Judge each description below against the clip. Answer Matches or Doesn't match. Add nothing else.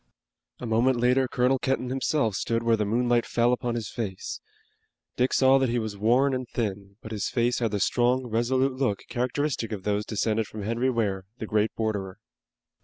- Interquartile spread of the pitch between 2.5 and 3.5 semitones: Matches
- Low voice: Matches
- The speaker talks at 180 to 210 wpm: Matches